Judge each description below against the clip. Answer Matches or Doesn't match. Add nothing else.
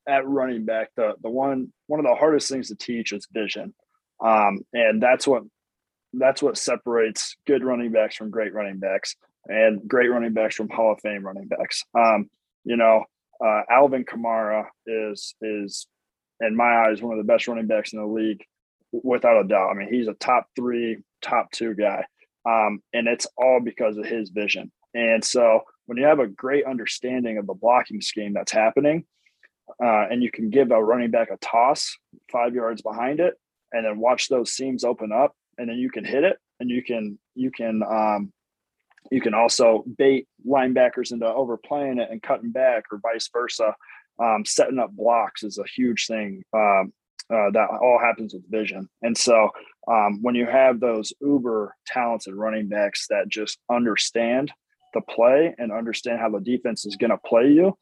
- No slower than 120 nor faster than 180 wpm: Doesn't match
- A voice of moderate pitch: Doesn't match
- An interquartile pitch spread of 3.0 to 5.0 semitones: Doesn't match